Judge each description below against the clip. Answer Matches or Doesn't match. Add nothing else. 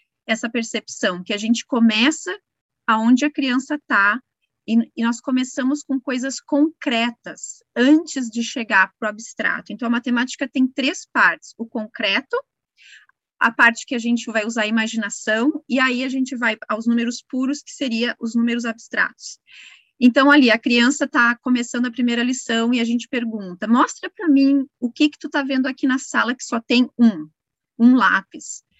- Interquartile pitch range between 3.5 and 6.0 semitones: Doesn't match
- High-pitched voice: Matches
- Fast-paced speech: Doesn't match